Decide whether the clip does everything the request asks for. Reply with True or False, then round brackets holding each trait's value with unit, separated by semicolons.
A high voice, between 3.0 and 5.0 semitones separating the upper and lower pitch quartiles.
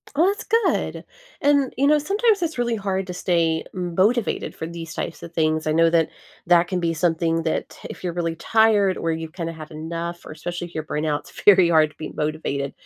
False (170 Hz; 4.0 semitones)